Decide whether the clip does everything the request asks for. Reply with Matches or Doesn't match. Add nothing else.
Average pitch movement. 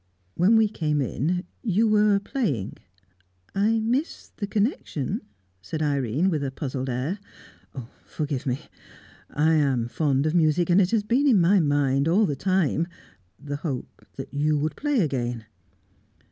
Doesn't match